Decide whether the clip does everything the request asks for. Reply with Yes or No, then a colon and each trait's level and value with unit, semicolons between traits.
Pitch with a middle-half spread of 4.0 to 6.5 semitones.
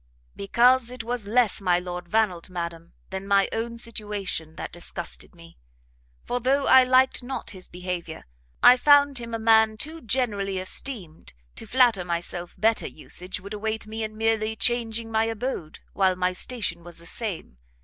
Yes: average, 4.6 semitones